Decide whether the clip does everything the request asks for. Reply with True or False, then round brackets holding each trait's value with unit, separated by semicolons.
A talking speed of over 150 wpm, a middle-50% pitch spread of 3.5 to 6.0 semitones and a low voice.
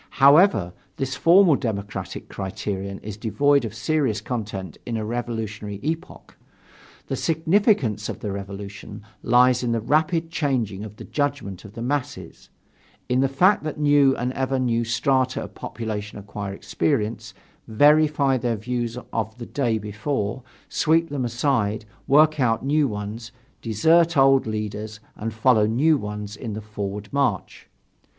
False (145 wpm; 5.1 semitones; 120 Hz)